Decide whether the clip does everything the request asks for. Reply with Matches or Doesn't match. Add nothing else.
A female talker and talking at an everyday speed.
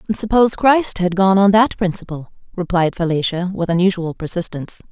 Matches